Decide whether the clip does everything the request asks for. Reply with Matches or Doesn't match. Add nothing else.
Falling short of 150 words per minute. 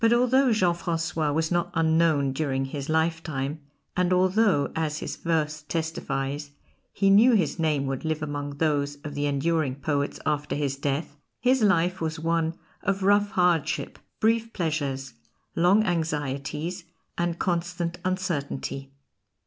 Matches